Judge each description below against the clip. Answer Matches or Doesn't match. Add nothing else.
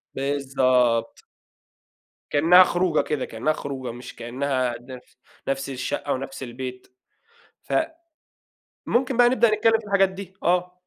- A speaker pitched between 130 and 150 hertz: Matches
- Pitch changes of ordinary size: Doesn't match